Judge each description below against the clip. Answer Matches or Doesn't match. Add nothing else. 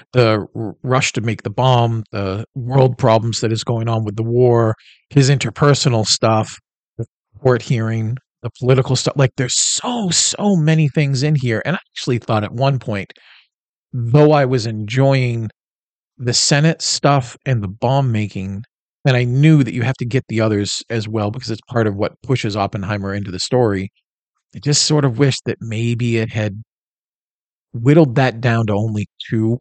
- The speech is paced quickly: Doesn't match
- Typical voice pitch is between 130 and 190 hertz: Doesn't match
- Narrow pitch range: Doesn't match